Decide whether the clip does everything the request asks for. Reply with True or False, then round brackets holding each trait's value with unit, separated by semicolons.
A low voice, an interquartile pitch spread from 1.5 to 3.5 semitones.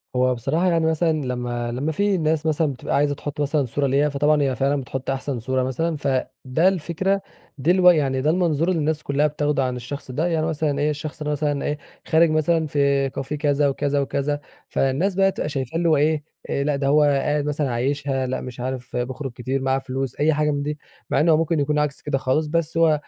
False (145 Hz; 2.6 semitones)